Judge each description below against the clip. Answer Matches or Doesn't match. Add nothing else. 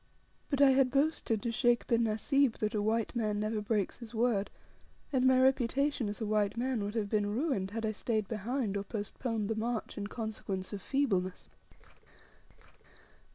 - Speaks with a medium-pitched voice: Doesn't match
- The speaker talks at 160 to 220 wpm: Matches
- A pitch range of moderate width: Matches